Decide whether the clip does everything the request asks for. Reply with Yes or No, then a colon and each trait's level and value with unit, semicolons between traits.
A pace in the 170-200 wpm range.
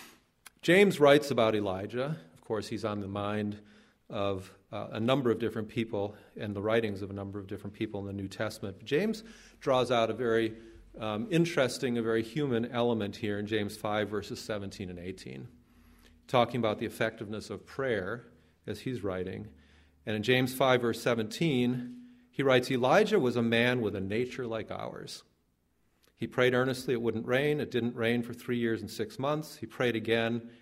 Yes: average, 180 wpm